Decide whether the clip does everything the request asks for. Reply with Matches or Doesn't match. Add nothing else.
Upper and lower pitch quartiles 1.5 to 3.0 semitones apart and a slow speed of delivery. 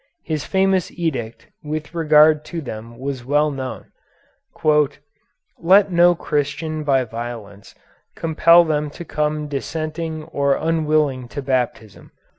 Doesn't match